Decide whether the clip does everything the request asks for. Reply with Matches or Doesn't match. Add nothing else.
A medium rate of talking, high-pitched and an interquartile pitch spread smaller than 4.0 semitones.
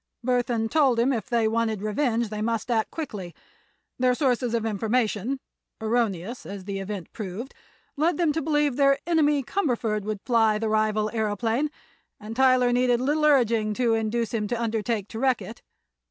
Matches